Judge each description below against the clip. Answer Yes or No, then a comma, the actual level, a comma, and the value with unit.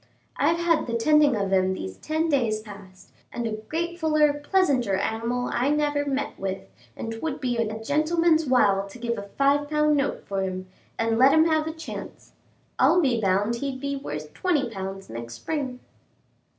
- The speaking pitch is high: Yes, very high, 255 Hz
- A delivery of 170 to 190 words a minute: Yes, average, 180 wpm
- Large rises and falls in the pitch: Yes, wide, 6.7 semitones